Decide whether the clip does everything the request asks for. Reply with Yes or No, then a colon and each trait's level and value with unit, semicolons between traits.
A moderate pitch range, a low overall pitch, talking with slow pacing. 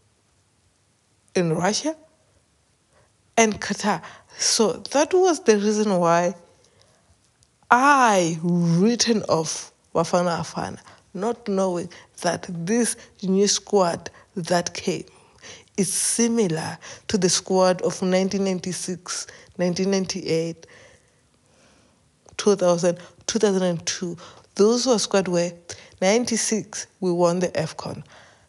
No: average, 3.7 semitones; medium, 185 Hz; slow, 90 wpm